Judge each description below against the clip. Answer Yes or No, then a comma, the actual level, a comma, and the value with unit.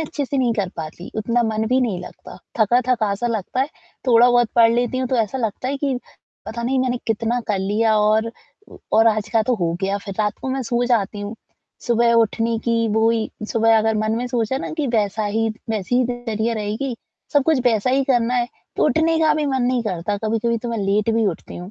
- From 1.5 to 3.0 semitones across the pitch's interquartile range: Yes, narrow, 2.5 semitones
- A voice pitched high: Yes, high, 230 Hz